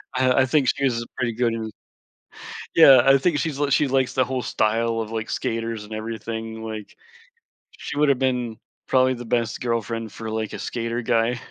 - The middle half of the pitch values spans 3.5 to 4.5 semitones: No, narrow, 2.5 semitones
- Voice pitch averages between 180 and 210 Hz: No, low, 115 Hz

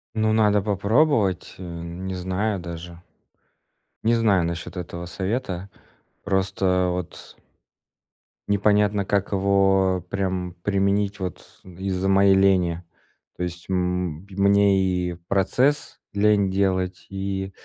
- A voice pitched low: Yes, very low, 95 Hz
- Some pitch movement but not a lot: No, narrow, 1.8 semitones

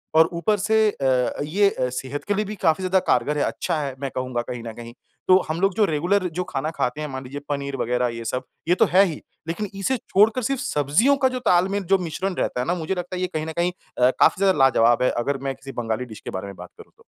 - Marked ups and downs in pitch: Yes, wide, 6.9 semitones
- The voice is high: No, medium, 155 Hz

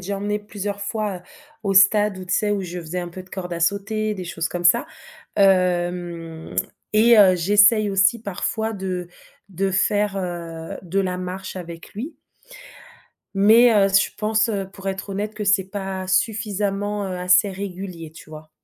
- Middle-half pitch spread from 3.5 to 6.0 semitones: No, narrow, 2.4 semitones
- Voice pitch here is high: Yes, high, 195 Hz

